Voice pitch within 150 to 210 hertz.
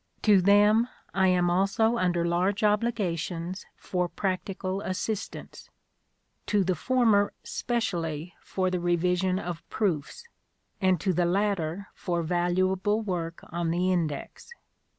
Yes: medium, 185 Hz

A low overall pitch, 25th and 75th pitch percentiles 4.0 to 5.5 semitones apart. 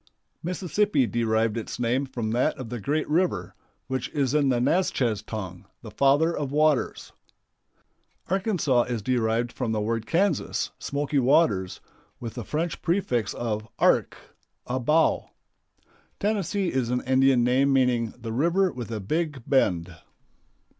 Yes: low, 130 Hz; average, 4.9 semitones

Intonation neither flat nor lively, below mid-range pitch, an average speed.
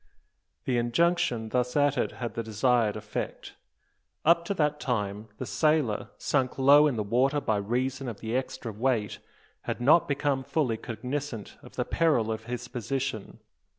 Yes: average, 4.2 semitones; low, 125 Hz; average, 155 wpm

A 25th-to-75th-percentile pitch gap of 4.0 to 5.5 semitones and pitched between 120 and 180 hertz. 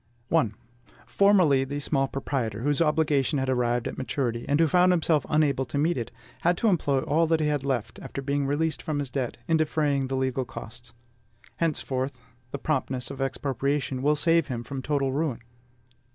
No: average, 2.9 semitones; medium, 140 Hz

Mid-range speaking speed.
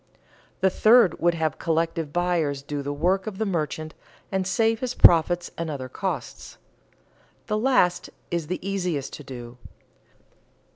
Yes: average, 145 wpm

